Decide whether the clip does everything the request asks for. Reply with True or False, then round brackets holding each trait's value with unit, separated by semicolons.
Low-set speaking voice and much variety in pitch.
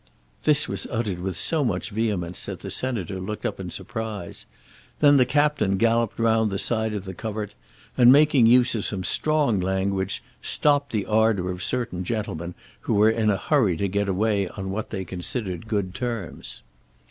False (105 Hz; 3.6 semitones)